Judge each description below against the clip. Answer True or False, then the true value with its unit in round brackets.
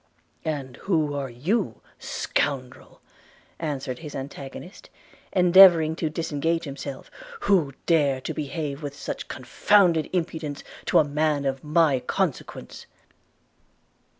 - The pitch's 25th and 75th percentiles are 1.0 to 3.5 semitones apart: True (3.2 semitones)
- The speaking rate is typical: False (110 wpm)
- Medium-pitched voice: True (150 Hz)